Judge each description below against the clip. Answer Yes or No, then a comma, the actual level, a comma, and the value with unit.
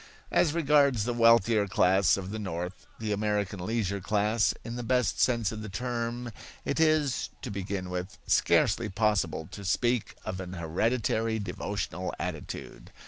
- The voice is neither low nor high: No, low, 105 Hz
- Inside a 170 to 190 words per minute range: No, average, 150 wpm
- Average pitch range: Yes, average, 3.9 semitones